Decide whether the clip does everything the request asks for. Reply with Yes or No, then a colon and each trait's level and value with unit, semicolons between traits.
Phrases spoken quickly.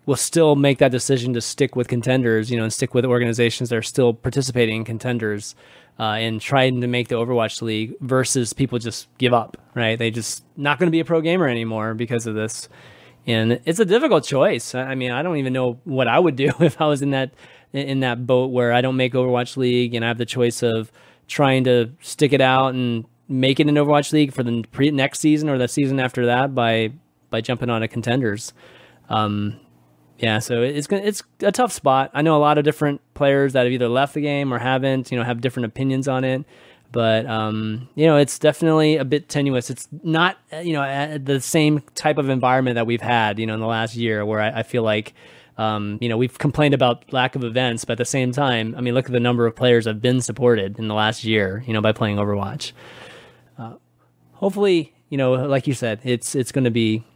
Yes: fast, 230 wpm